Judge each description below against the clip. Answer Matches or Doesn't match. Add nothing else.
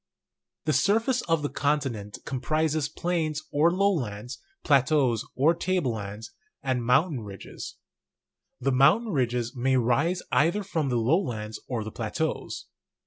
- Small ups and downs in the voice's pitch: Doesn't match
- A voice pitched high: Doesn't match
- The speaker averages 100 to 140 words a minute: Matches